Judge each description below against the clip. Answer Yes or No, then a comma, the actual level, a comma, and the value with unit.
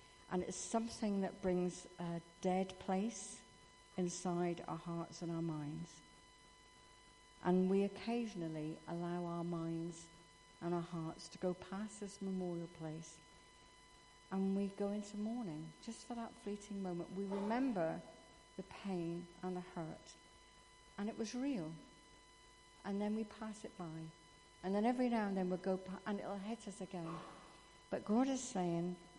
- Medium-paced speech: Yes, average, 155 wpm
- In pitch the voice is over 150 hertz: Yes, medium, 185 Hz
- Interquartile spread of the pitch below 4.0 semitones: Yes, average, 3.2 semitones